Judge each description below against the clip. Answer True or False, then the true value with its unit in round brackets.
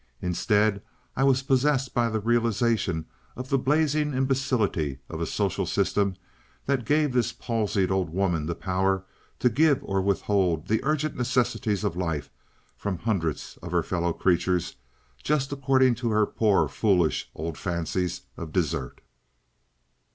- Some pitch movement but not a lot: False (6.2 semitones)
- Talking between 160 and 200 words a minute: False (145 wpm)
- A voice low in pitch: True (105 Hz)